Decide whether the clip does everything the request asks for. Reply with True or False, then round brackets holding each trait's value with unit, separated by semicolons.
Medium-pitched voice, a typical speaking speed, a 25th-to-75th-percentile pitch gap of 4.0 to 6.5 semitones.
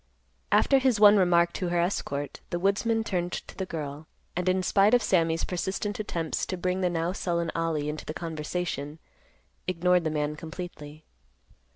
False (175 Hz; 170 wpm; 2.9 semitones)